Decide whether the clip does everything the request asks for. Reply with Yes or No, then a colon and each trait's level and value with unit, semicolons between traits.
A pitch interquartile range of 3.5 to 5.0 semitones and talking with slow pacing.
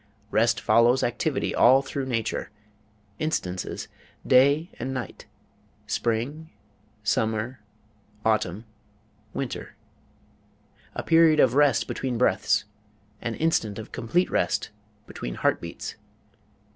Yes: average, 4.0 semitones; slow, 100 wpm